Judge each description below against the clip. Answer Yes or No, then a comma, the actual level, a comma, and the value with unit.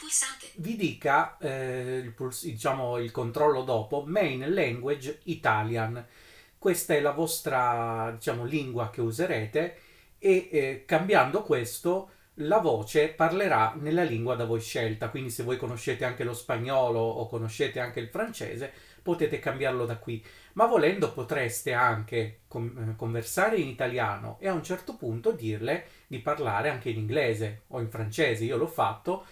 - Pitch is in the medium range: No, low, 125 Hz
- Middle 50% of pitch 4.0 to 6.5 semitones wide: Yes, average, 5.1 semitones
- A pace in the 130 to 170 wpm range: Yes, average, 145 wpm